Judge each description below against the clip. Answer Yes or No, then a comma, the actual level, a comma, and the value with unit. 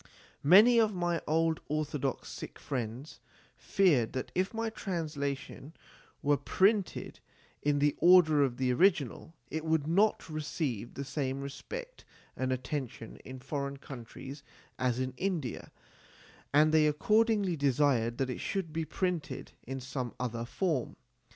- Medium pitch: Yes, medium, 145 Hz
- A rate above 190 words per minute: No, slow, 135 wpm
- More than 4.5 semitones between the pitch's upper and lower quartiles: Yes, average, 4.9 semitones